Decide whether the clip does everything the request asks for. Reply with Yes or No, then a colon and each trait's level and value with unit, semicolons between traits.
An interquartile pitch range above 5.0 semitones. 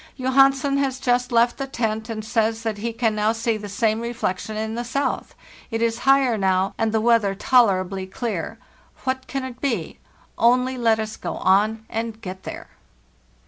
No: narrow, 2.5 semitones